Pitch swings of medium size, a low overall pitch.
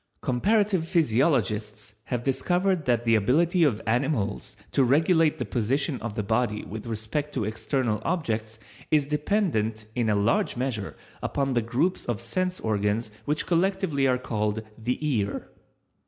No: wide, 5.7 semitones; low, 125 Hz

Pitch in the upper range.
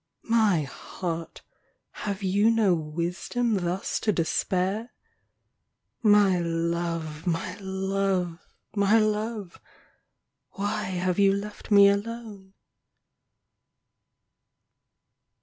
Yes: high, 195 Hz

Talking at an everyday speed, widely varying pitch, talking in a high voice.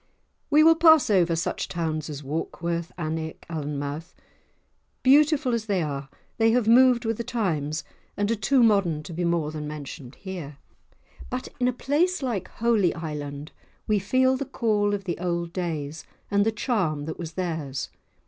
No: average, 165 wpm; wide, 7.0 semitones; medium, 180 Hz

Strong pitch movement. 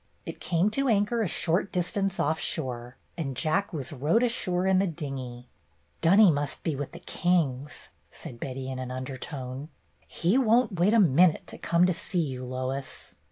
Yes: wide, 6.3 semitones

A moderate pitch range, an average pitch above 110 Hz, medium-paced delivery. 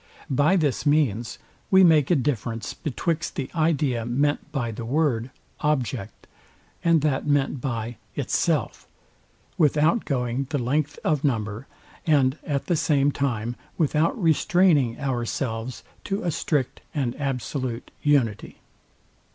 No: average, 4.0 semitones; medium, 140 Hz; slow, 125 wpm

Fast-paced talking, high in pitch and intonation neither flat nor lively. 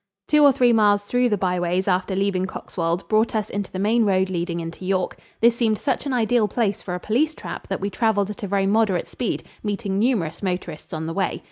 Yes: fast, 225 wpm; high, 200 Hz; average, 3.4 semitones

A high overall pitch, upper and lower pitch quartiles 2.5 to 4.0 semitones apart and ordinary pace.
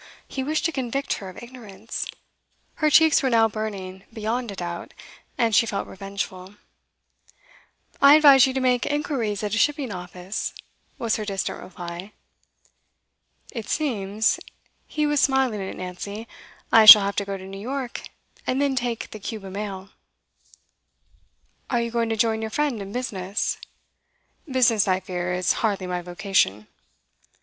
No: high, 215 Hz; average, 4.8 semitones; average, 155 wpm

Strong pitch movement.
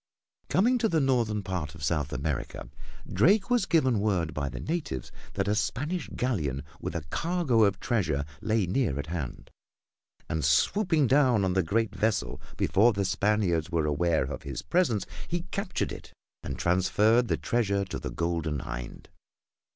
Yes: wide, 8.0 semitones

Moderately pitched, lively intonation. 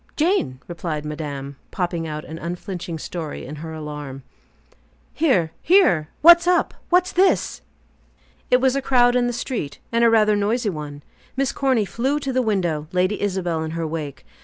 Yes: medium, 180 Hz; wide, 8.4 semitones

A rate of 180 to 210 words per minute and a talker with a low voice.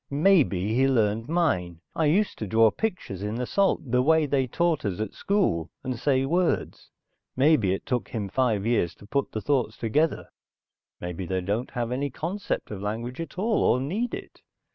Yes: average, 185 wpm; low, 125 Hz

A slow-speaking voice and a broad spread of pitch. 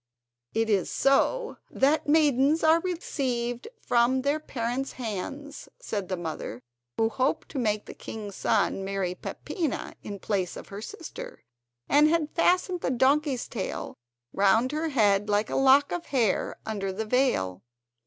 No: average, 150 wpm; wide, 6.2 semitones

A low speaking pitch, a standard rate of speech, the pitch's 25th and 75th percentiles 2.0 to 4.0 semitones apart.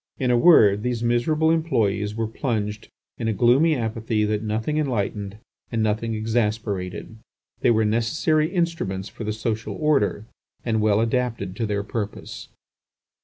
Yes: low, 110 Hz; average, 145 wpm; average, 2.8 semitones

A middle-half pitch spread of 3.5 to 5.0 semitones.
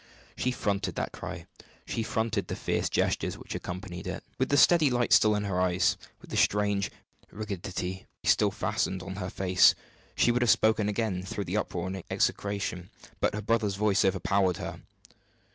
No: average, 2.8 semitones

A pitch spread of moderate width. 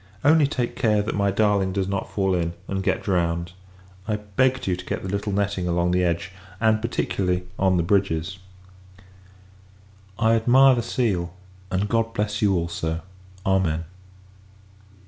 Yes: average, 3.4 semitones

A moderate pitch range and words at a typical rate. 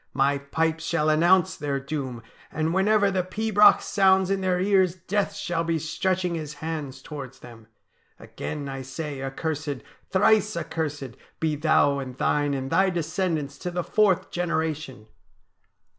Yes: average, 4.7 semitones; average, 145 wpm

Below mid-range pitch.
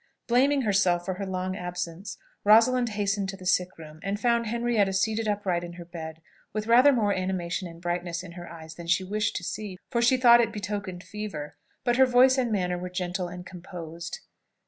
No: high, 190 Hz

